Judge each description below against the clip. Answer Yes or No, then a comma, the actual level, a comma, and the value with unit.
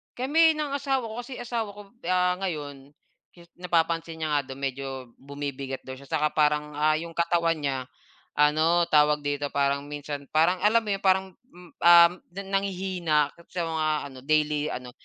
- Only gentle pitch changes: No, average, 4.2 semitones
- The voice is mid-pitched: Yes, medium, 160 Hz